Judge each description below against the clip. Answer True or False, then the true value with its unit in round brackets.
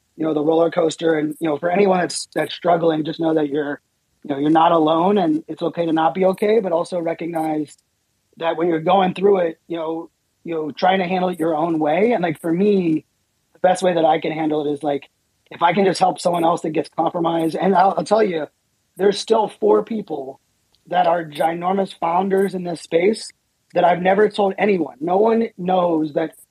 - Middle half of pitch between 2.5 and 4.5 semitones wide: True (2.9 semitones)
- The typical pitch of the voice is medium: True (165 Hz)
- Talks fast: True (220 wpm)